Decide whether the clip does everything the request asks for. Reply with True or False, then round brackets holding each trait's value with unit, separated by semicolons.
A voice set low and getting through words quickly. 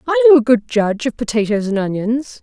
False (240 Hz; 225 wpm)